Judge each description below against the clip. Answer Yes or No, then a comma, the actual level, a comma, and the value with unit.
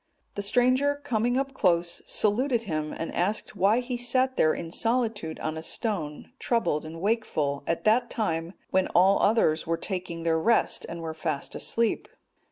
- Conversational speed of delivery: Yes, average, 170 wpm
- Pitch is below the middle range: No, high, 200 Hz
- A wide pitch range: Yes, wide, 6.2 semitones